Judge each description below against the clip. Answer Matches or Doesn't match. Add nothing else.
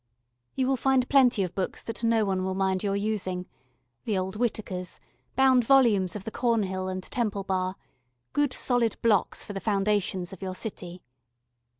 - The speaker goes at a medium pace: Matches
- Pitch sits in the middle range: Doesn't match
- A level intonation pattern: Doesn't match